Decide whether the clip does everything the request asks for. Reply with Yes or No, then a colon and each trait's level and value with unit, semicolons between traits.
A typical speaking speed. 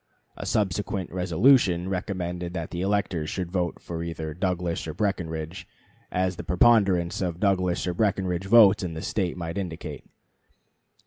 Yes: average, 155 wpm